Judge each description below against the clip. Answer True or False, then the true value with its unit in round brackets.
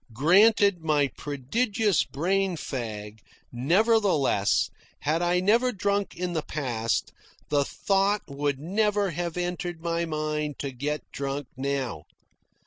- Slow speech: True (120 wpm)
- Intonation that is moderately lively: False (5.8 semitones)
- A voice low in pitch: False (160 Hz)